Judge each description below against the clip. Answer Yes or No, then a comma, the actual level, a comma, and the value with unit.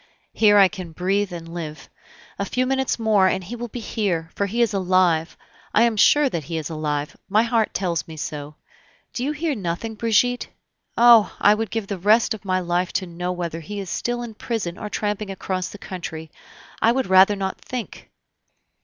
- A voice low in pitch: No, high, 195 Hz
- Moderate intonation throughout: Yes, average, 4.5 semitones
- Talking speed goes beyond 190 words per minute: Yes, average, 200 wpm